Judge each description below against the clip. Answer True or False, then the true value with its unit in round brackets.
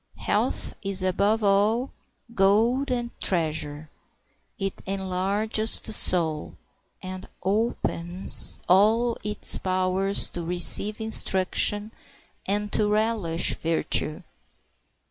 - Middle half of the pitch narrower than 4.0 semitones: True (2.9 semitones)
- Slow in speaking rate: True (90 wpm)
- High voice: True (195 Hz)